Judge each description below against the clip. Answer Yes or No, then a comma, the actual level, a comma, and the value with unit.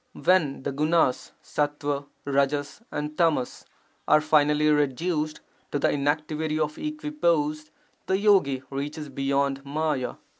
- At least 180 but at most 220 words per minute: No, slow, 135 wpm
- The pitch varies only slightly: Yes, narrow, 2.0 semitones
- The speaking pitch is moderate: Yes, medium, 150 Hz